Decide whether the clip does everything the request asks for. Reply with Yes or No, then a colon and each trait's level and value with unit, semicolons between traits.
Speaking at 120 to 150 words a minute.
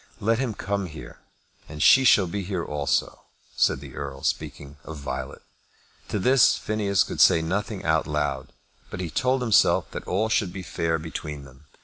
No: average, 175 wpm